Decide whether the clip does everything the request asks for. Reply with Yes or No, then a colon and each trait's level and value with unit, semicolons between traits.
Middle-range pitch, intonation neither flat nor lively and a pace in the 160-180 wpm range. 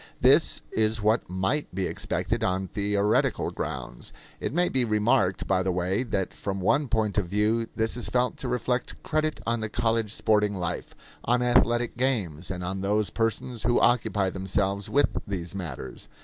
No: low, 105 Hz; average, 3.8 semitones; average, 170 wpm